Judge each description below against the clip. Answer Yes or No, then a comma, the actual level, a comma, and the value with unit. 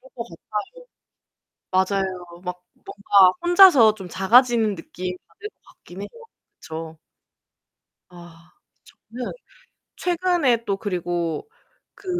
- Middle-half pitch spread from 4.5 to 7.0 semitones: Yes, wide, 5.4 semitones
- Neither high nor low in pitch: No, high, 195 Hz